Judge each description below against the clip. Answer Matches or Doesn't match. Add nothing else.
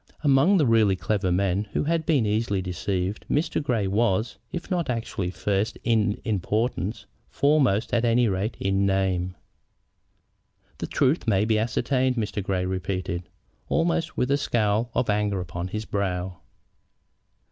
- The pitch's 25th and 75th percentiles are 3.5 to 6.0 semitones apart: Matches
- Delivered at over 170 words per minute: Doesn't match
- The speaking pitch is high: Doesn't match